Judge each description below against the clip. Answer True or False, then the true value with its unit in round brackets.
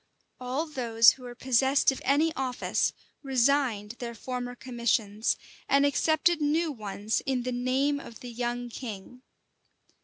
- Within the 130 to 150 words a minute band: True (135 wpm)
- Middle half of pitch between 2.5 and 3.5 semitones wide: True (2.9 semitones)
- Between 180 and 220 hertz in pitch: False (250 Hz)